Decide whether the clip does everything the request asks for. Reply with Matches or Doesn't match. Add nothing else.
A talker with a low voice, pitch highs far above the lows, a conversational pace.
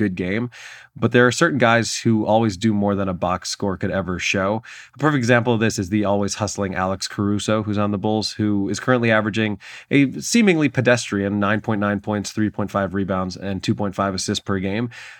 Doesn't match